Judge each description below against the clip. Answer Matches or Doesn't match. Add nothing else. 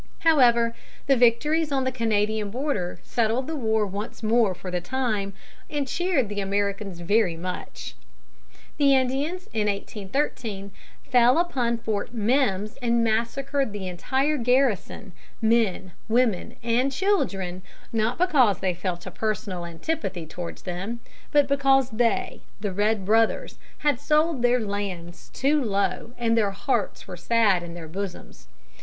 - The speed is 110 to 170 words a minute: Matches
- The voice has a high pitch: Matches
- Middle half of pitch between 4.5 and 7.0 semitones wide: Matches